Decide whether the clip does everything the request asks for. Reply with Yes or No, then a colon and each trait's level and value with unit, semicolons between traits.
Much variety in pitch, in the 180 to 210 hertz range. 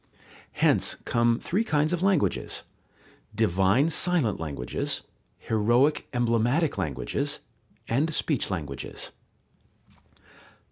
No: wide, 7.5 semitones; low, 120 Hz